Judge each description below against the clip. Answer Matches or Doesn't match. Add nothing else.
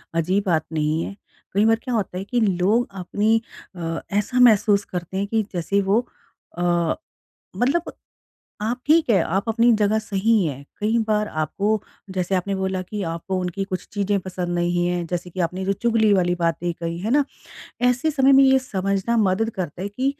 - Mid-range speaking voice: Doesn't match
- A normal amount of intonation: Matches